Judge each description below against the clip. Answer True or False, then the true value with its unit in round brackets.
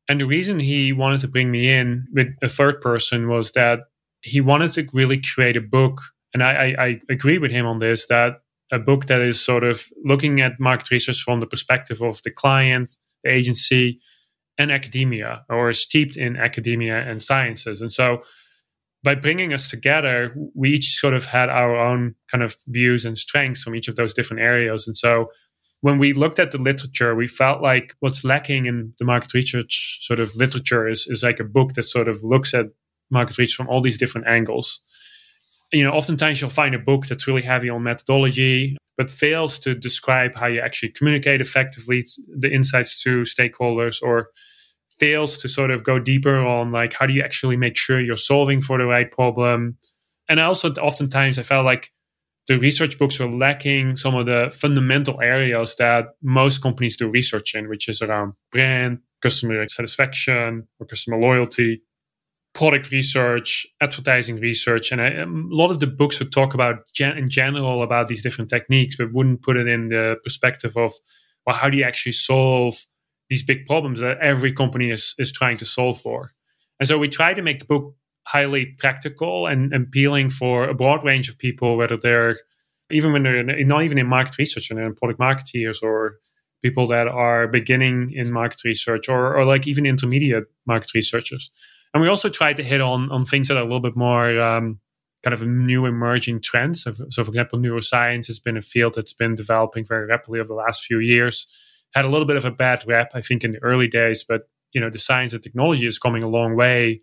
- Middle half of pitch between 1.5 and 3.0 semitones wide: True (2.5 semitones)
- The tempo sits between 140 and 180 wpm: False (200 wpm)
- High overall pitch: False (125 Hz)